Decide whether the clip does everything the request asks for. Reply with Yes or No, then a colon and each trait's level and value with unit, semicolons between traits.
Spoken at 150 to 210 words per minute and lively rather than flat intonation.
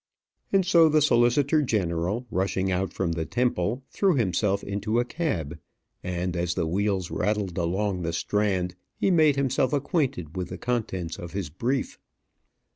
Yes: average, 155 wpm; wide, 6.4 semitones